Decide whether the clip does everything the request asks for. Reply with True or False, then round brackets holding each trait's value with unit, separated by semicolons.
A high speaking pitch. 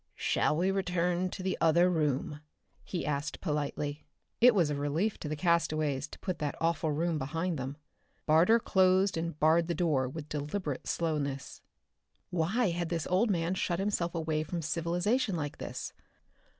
False (165 Hz)